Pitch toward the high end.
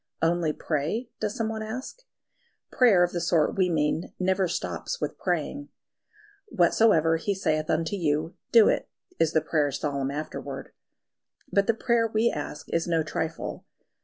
No: medium, 170 Hz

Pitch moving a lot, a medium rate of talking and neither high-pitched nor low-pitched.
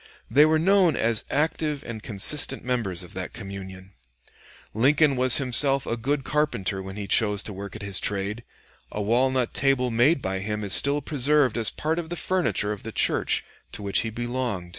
No: wide, 5.9 semitones; average, 185 wpm; low, 120 Hz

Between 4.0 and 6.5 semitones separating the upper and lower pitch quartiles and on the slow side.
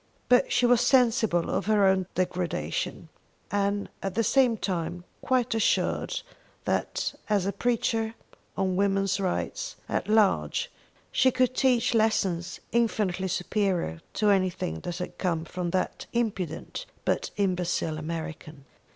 Yes: average, 4.3 semitones; slow, 130 wpm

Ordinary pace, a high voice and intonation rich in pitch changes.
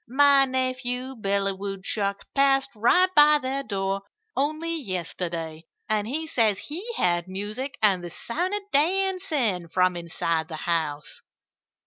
No: slow, 130 wpm; high, 225 Hz; wide, 7.3 semitones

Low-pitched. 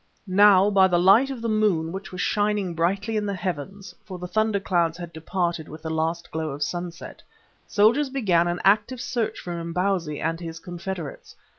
No: medium, 180 Hz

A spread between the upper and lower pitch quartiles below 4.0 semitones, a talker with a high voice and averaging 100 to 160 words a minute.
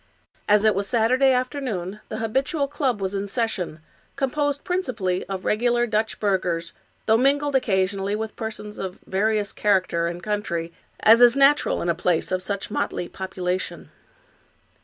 No: average, 4.8 semitones; high, 210 Hz; average, 150 wpm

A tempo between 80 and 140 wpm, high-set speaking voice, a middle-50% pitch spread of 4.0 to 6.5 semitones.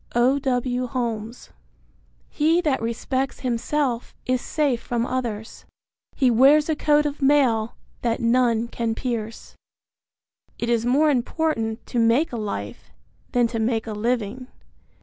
No: slow, 135 wpm; high, 245 Hz; average, 2.9 semitones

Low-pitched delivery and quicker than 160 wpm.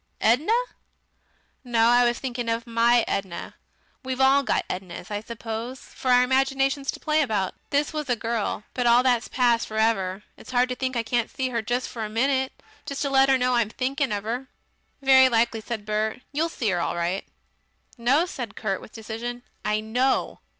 No: high, 240 Hz; average, 190 wpm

